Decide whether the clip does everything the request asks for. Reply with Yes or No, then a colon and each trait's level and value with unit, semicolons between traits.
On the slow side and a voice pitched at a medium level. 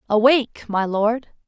No: slow, 120 wpm; high, 225 Hz